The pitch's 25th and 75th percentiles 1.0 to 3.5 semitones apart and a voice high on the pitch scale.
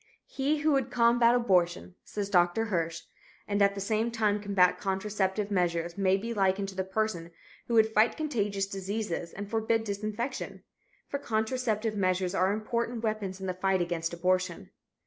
Yes: average, 3.1 semitones; high, 200 Hz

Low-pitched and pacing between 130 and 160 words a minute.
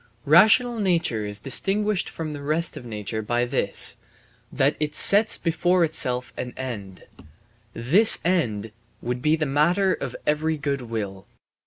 No: medium, 145 Hz; average, 145 wpm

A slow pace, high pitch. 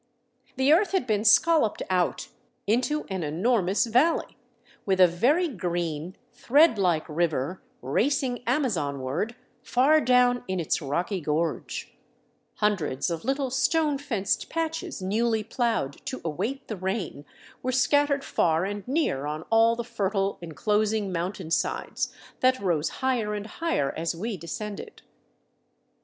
Yes: slow, 130 wpm; high, 210 Hz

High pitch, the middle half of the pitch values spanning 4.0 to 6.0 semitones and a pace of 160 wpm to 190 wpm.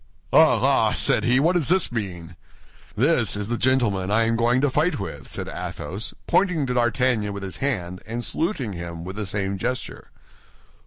No: low, 115 Hz; average, 5.0 semitones; average, 180 wpm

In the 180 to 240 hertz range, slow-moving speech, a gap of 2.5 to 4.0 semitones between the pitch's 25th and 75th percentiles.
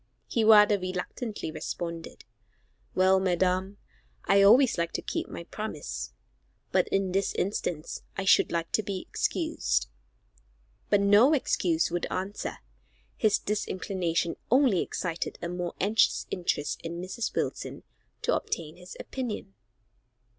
Yes: medium, 185 Hz; slow, 125 wpm; average, 3.4 semitones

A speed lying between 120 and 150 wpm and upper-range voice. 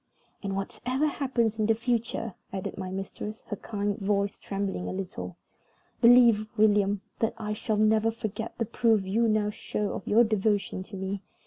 No: average, 165 wpm; high, 210 Hz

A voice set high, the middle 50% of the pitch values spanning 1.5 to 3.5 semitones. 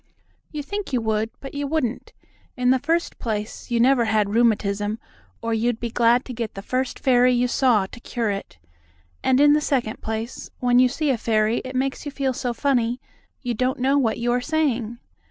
Yes: high, 245 Hz; average, 2.9 semitones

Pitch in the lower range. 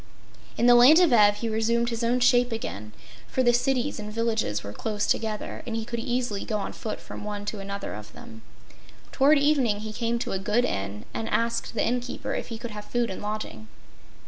No: high, 225 Hz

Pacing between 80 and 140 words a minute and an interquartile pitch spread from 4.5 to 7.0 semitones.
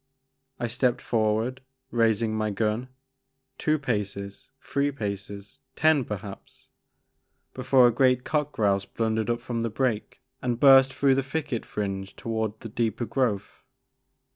No: slow, 135 wpm; average, 3.6 semitones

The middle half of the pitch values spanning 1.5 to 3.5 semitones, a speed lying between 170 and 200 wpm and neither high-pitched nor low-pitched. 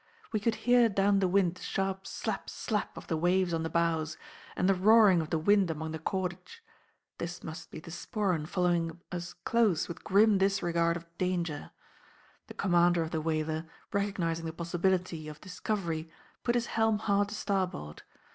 Yes: average, 3.2 semitones; average, 175 wpm; medium, 180 Hz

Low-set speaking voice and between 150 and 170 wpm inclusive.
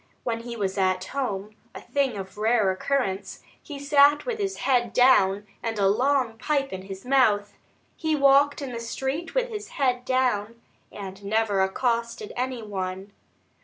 No: high, 235 Hz; average, 165 wpm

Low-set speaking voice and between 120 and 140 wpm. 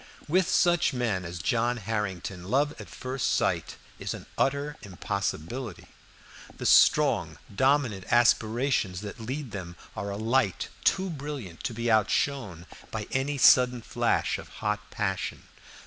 Yes: low, 115 Hz; slow, 135 wpm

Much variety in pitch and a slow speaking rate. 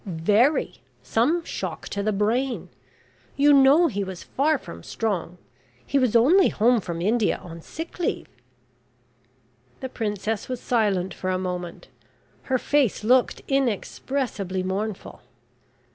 Yes: wide, 5.8 semitones; slow, 130 wpm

